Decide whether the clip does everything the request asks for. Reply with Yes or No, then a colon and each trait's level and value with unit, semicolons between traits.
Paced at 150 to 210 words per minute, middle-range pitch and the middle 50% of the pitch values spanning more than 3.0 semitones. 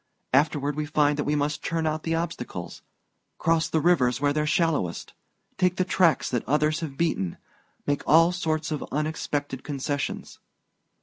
No: average, 165 wpm; medium, 150 Hz; narrow, 2.4 semitones